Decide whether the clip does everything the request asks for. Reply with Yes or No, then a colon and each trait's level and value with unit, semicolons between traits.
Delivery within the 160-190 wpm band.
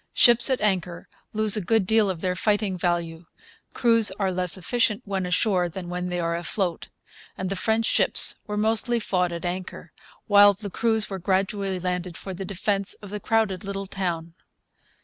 Yes: average, 180 wpm